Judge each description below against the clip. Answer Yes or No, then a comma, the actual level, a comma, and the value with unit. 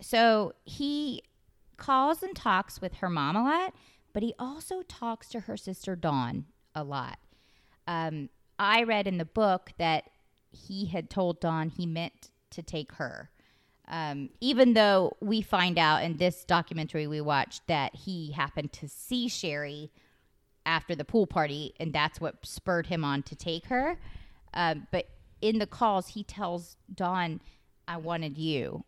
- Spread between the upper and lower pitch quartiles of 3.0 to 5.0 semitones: No, wide, 5.6 semitones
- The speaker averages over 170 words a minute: No, average, 160 wpm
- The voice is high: No, medium, 175 Hz